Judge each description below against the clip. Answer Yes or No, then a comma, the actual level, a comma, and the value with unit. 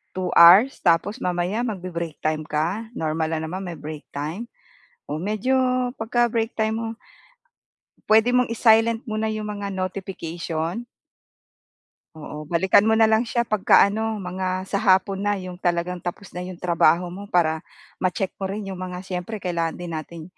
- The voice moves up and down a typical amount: Yes, average, 4.1 semitones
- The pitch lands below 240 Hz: Yes, medium, 185 Hz